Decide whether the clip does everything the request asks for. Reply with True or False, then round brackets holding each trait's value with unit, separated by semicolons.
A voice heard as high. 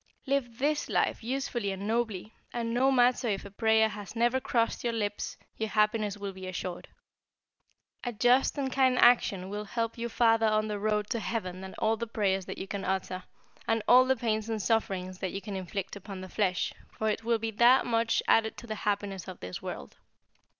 True (220 Hz)